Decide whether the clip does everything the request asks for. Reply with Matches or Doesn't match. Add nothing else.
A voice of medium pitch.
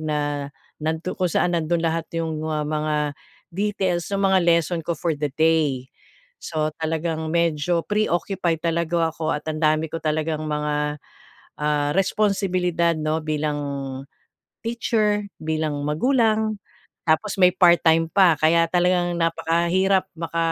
Matches